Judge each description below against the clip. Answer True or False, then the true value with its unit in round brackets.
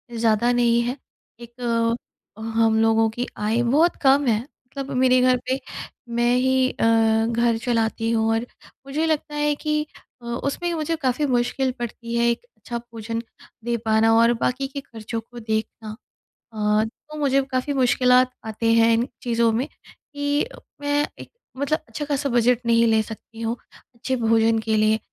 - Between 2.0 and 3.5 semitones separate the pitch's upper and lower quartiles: True (3.0 semitones)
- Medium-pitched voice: False (240 Hz)